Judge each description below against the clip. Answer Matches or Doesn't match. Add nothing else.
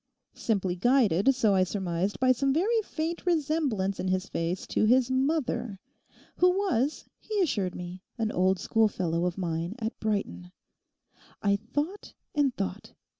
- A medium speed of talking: Matches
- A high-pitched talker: Matches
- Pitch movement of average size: Doesn't match